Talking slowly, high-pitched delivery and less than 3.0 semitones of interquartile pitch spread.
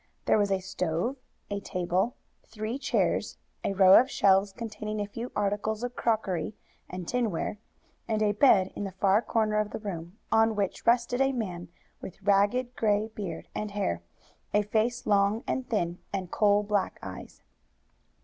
No: average, 165 wpm; high, 205 Hz; narrow, 2.5 semitones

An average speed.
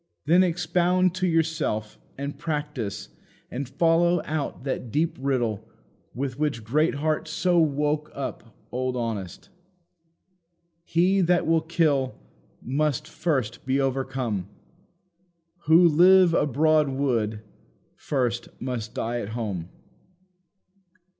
No: slow, 105 wpm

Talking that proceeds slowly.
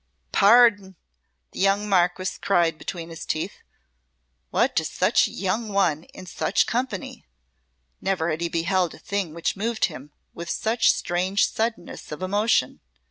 No: average, 145 wpm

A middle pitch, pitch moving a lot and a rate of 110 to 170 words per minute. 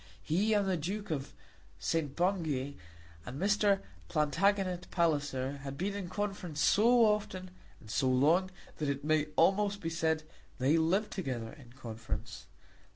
Yes: medium, 165 Hz; wide, 5.8 semitones; average, 145 wpm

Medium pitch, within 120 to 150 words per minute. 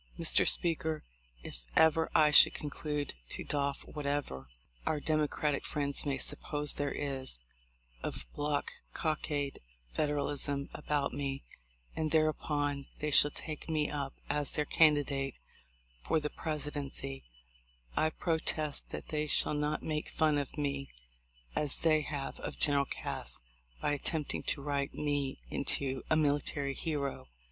Yes: medium, 145 Hz; slow, 135 wpm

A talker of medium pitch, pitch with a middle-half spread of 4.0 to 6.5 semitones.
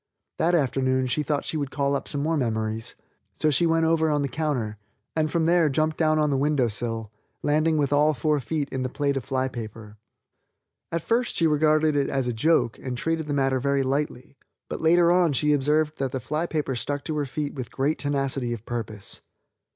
No: medium, 145 Hz; average, 3.1 semitones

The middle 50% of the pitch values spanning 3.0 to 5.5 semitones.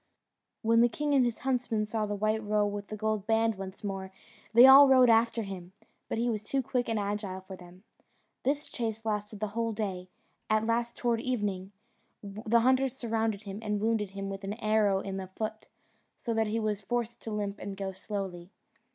No: narrow, 2.5 semitones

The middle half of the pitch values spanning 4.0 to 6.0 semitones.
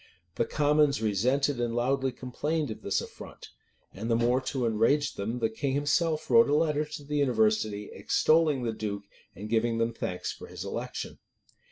Yes: average, 4.5 semitones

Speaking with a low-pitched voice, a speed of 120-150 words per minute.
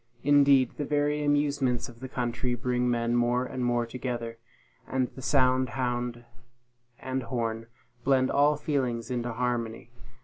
Yes: low, 125 Hz; average, 140 wpm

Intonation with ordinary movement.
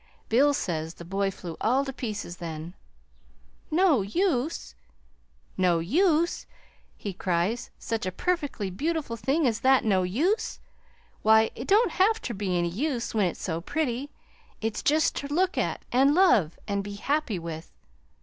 No: wide, 8.1 semitones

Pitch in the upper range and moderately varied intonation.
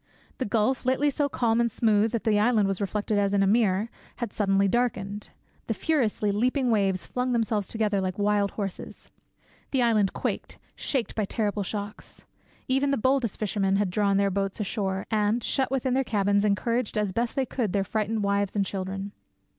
Yes: high, 210 Hz; average, 3.0 semitones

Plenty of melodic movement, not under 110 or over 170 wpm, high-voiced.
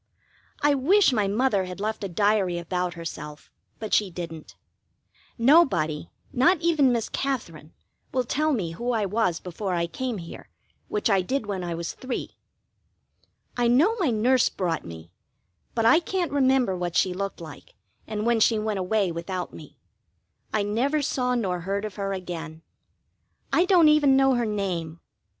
Yes: wide, 6.4 semitones; average, 165 wpm; high, 210 Hz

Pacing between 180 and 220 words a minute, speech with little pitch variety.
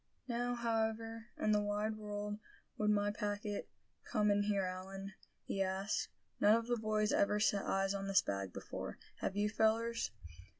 No: average, 165 wpm; narrow, 1.7 semitones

